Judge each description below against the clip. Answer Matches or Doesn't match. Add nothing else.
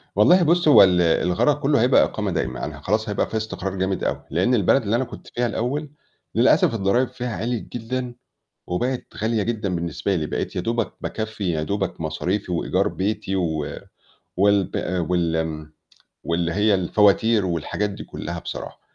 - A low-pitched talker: Matches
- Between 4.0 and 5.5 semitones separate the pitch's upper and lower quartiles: Matches